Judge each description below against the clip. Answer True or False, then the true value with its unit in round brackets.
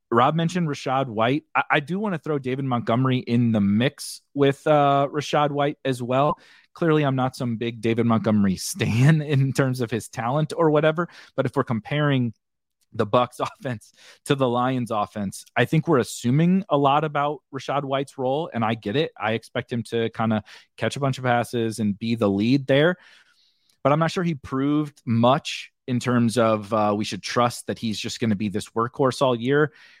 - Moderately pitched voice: False (130 Hz)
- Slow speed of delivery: False (200 wpm)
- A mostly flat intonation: False (4.1 semitones)